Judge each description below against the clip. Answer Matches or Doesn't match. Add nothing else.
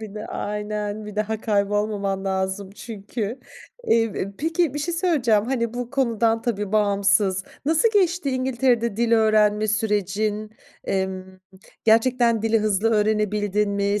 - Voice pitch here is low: Doesn't match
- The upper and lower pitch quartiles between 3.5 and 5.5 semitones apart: Doesn't match